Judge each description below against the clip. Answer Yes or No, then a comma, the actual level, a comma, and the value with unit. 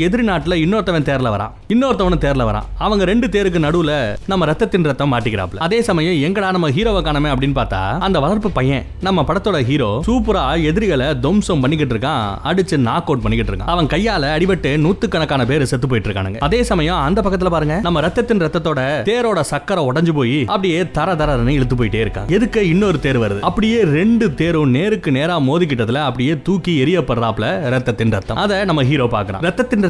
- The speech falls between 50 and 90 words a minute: Yes, slow, 75 wpm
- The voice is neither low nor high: Yes, medium, 155 Hz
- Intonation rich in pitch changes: Yes, wide, 6.6 semitones